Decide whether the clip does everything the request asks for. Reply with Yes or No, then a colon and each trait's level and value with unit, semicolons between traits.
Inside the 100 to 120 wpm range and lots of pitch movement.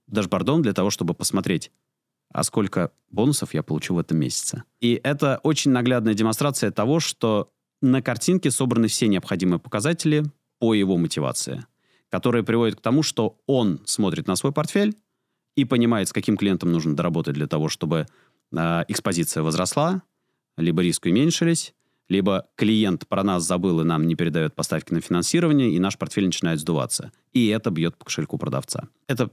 No: fast, 160 wpm; wide, 7.8 semitones